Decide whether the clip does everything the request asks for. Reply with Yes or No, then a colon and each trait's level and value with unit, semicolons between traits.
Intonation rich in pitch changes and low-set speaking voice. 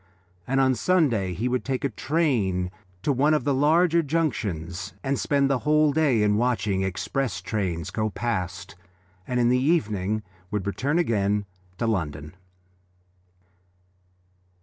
Yes: wide, 6.3 semitones; low, 120 Hz